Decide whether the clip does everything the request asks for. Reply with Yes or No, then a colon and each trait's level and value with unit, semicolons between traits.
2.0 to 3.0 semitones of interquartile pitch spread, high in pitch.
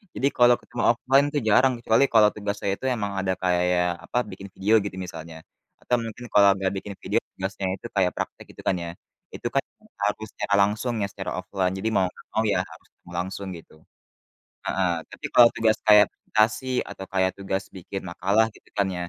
No: average, 2.7 semitones; low, 100 Hz